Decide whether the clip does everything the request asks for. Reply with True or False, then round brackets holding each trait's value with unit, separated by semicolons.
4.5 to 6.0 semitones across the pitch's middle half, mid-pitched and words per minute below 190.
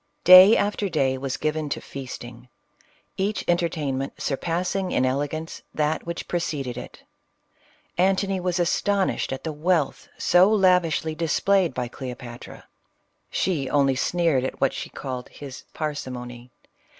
True (5.3 semitones; 155 Hz; 140 wpm)